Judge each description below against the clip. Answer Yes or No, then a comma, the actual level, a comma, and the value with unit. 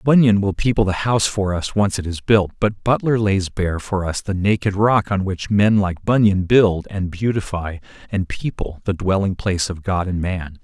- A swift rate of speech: Yes, fast, 210 wpm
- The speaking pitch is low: Yes, very low, 95 Hz